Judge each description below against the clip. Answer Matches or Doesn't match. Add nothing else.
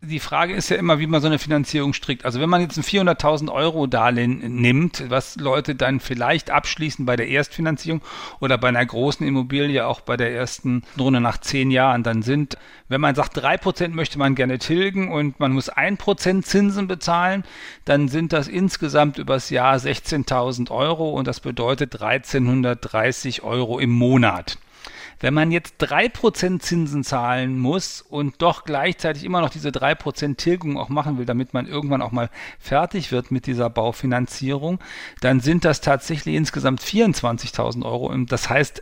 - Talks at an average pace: Matches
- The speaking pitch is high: Doesn't match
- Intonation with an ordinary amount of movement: Matches